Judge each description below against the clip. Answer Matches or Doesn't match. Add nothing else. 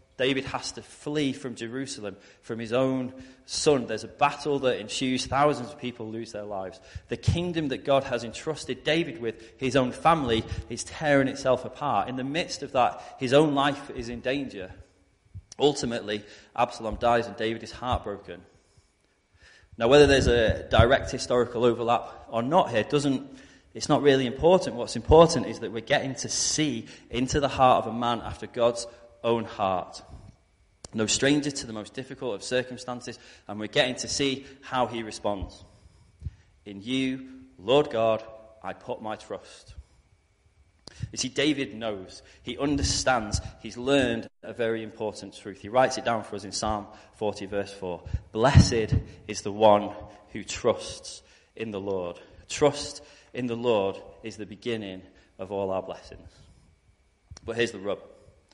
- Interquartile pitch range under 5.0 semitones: Matches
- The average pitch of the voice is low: Matches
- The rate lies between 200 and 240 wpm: Doesn't match